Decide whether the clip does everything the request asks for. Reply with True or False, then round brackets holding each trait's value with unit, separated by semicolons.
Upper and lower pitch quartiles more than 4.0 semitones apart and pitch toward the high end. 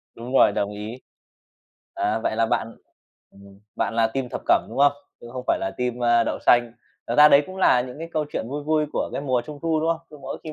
False (4.7 semitones; 125 Hz)